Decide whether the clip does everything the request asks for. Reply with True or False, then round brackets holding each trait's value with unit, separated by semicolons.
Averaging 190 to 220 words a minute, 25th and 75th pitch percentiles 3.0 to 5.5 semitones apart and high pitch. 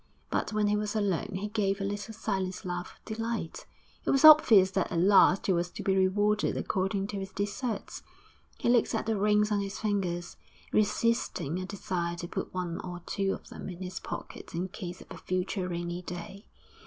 False (200 wpm; 2.5 semitones; 195 Hz)